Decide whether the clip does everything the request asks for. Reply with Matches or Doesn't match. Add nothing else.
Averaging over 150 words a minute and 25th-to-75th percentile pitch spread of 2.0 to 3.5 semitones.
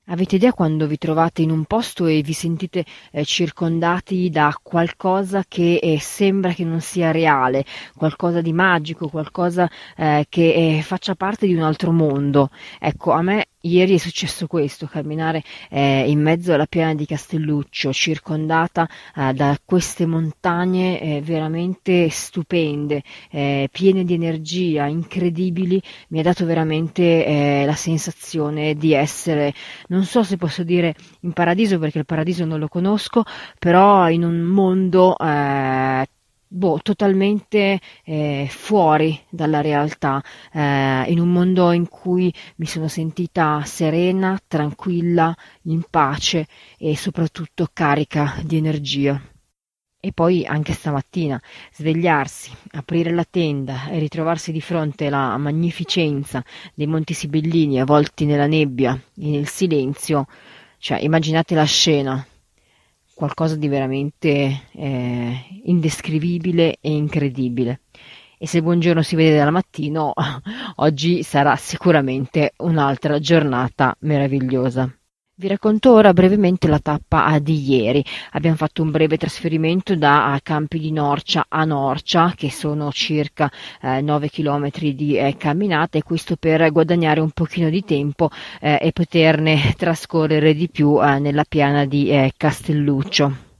Doesn't match